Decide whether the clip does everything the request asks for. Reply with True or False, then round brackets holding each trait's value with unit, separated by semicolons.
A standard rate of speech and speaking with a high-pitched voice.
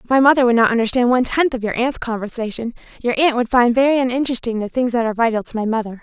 False (250 wpm; 240 Hz)